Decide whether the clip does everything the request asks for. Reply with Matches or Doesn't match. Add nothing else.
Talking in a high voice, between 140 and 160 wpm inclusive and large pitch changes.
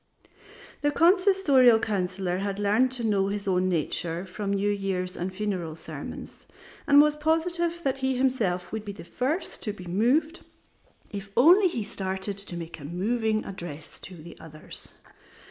Matches